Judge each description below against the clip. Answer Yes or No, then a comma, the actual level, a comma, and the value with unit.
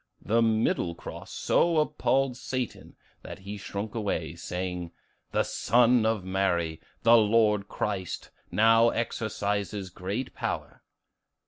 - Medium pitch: No, low, 105 Hz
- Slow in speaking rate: Yes, slow, 115 wpm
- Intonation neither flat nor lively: Yes, average, 3.3 semitones